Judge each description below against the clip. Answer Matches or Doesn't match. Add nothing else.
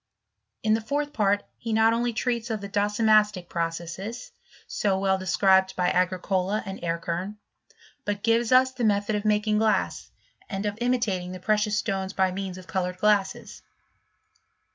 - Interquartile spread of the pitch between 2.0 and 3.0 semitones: Matches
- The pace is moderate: Matches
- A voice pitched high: Matches